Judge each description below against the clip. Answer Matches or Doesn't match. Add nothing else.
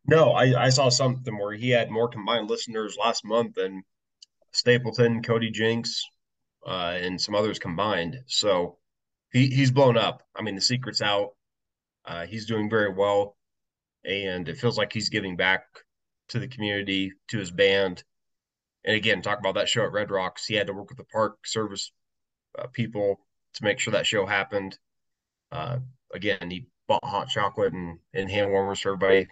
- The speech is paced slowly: Doesn't match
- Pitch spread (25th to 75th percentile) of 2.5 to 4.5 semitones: Matches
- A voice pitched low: Matches